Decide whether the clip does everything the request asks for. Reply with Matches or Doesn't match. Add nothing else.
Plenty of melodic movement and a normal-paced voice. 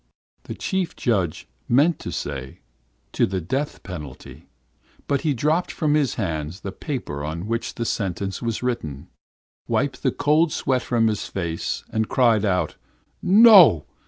Matches